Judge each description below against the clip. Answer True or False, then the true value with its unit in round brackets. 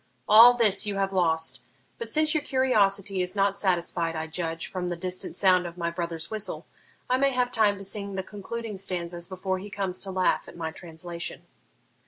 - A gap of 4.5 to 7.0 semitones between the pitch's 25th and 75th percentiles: False (3.2 semitones)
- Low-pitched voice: False (190 Hz)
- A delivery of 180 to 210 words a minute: True (195 wpm)